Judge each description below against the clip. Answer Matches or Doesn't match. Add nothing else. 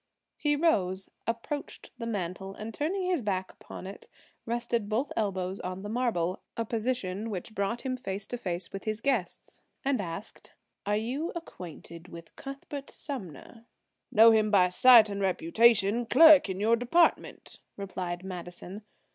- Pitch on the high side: Matches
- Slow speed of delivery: Doesn't match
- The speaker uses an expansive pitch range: Doesn't match